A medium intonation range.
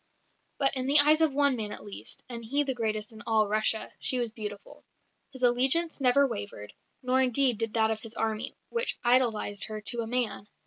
Yes: average, 3.4 semitones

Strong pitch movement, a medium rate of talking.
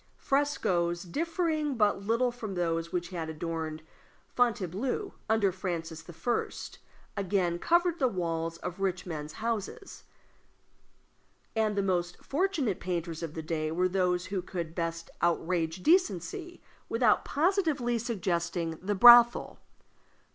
No: wide, 6.1 semitones; slow, 120 wpm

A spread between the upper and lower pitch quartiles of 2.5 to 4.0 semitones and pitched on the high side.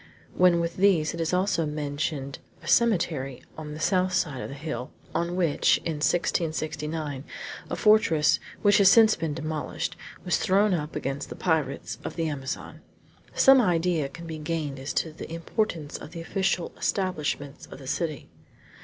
No: average, 3.4 semitones; medium, 160 Hz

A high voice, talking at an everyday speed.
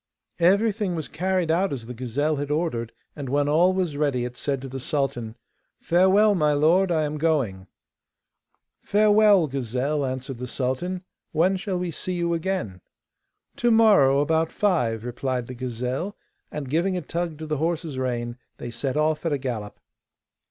No: medium, 150 Hz; average, 165 wpm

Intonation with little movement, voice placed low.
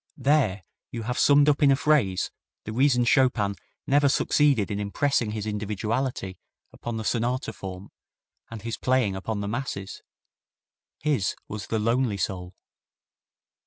No: average, 4.7 semitones; low, 115 Hz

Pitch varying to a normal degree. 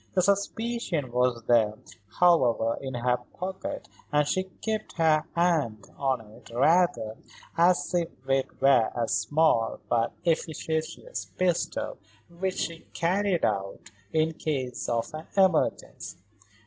No: wide, 6.6 semitones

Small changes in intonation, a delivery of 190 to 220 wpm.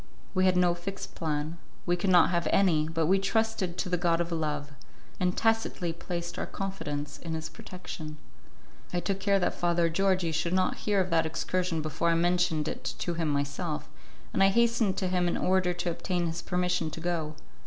Yes: narrow, 2.3 semitones; average, 195 wpm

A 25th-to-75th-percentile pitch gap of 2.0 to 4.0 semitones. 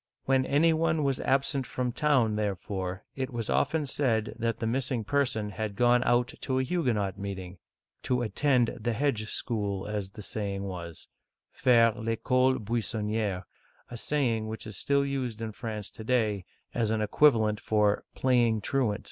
Yes: average, 3.6 semitones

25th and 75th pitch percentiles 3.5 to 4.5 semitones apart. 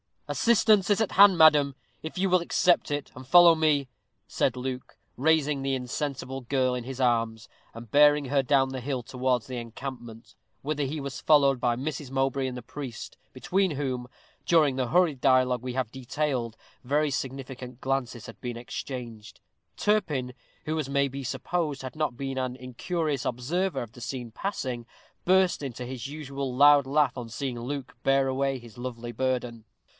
No: average, 2.9 semitones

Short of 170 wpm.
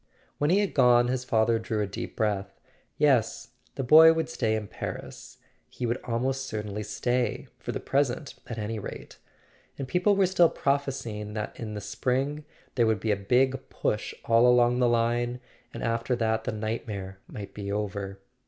No: average, 175 wpm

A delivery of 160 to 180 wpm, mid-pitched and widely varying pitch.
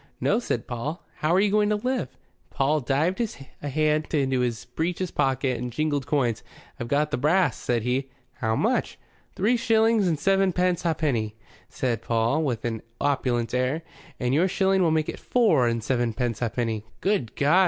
Yes: average, 175 wpm; medium, 145 Hz; wide, 6.7 semitones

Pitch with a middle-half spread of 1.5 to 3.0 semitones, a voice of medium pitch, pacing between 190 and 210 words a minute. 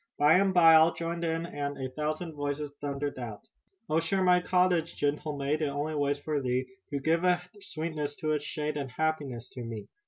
Yes: narrow, 2.4 semitones; medium, 150 Hz; average, 195 wpm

